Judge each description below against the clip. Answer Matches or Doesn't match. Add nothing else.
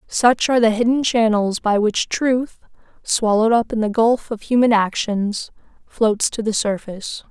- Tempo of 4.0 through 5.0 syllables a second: Matches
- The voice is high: Matches